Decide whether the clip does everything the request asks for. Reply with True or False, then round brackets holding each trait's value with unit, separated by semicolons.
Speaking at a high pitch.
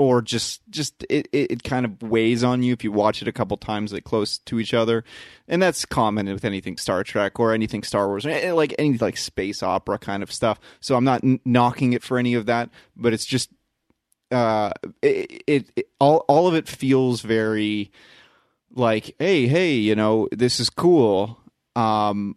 False (120 Hz)